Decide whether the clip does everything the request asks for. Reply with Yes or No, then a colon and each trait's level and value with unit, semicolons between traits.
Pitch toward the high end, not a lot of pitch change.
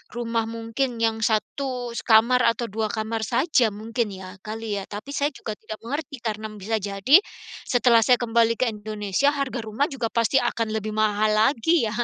Yes: high, 225 Hz; narrow, 2.3 semitones